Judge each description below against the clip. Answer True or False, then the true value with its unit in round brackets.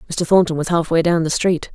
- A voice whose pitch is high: False (165 Hz)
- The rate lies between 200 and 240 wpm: False (275 wpm)